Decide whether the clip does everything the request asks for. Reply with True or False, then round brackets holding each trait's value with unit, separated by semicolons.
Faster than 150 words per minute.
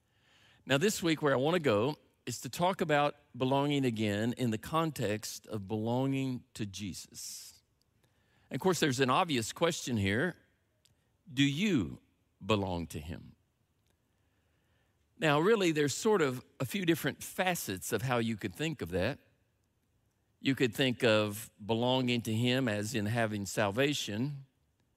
False (145 wpm)